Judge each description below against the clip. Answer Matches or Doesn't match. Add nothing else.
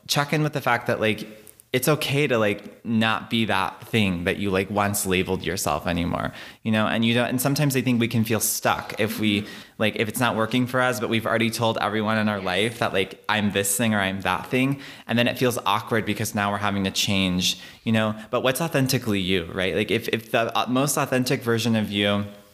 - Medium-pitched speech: Doesn't match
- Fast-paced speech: Matches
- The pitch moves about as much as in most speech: Matches